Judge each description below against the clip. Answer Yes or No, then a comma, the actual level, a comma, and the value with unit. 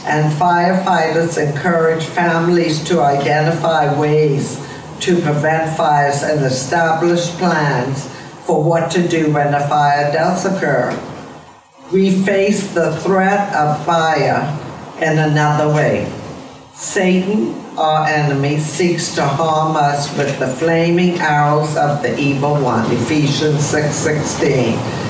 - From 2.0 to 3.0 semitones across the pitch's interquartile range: Yes, narrow, 2.6 semitones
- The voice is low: No, medium, 155 Hz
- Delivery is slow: Yes, slow, 115 wpm